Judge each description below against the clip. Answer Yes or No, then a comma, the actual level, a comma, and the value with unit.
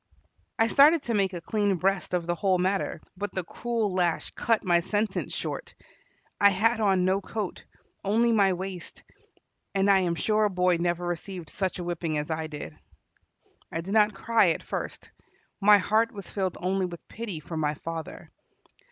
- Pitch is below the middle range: No, high, 190 Hz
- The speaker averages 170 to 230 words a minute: Yes, average, 180 wpm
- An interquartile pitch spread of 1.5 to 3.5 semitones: Yes, average, 3.1 semitones